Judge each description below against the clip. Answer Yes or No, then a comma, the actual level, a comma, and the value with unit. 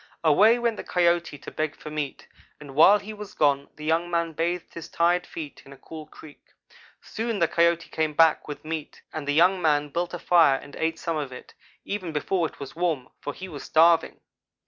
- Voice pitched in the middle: Yes, medium, 165 Hz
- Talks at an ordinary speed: No, fast, 210 wpm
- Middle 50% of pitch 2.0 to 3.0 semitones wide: Yes, narrow, 2.6 semitones